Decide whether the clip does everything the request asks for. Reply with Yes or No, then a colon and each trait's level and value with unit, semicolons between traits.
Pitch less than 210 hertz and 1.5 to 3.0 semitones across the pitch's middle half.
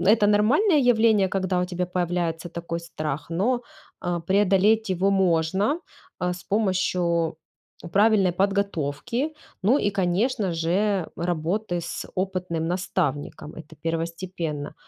No: medium, 185 Hz; average, 3.5 semitones